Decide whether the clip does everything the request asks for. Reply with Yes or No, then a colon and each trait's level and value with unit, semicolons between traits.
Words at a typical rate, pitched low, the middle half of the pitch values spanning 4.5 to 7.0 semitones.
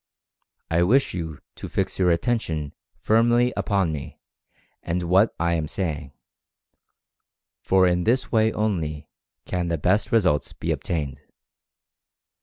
No: slow, 125 wpm; very low, 90 Hz; average, 5.2 semitones